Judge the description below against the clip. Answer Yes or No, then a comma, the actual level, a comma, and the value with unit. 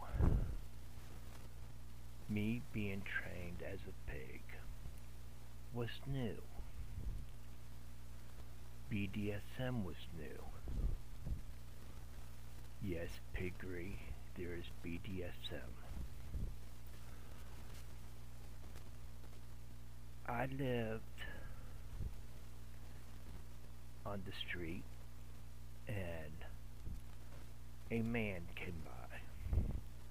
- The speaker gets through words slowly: Yes, slow, 50 wpm